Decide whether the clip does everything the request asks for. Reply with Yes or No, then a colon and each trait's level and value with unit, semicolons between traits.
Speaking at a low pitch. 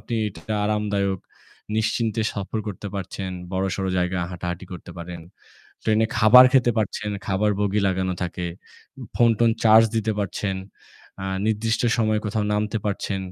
Yes: low, 105 Hz